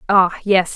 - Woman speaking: Yes, female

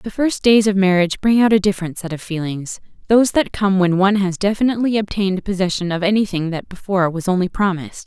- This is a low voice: No, high, 195 Hz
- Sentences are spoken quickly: Yes, fast, 210 wpm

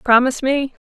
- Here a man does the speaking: No, female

